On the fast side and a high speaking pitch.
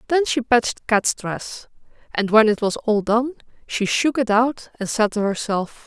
No: average, 195 wpm; high, 225 Hz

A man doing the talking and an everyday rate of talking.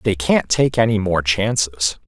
Yes: male; average, 175 wpm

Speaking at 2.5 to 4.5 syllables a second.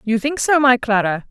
No: 5.0 syllables/s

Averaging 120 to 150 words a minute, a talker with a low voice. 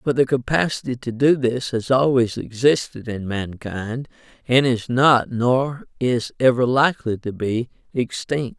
Yes: average, 145 wpm; low, 125 Hz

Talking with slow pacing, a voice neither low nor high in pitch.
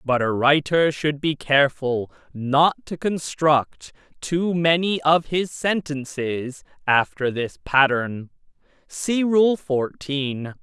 Yes: slow, 115 wpm; medium, 145 Hz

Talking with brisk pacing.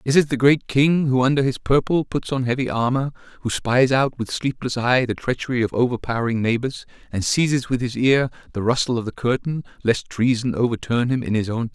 Yes: fast, 215 wpm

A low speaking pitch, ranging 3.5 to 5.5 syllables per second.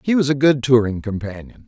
No: low, 125 Hz; 5.7 syllables/s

